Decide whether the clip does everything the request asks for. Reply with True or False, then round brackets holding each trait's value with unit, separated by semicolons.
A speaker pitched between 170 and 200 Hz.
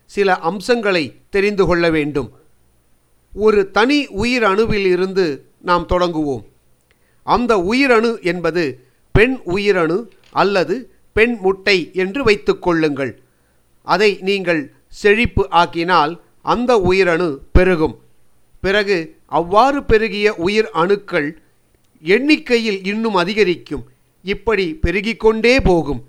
True (190 Hz)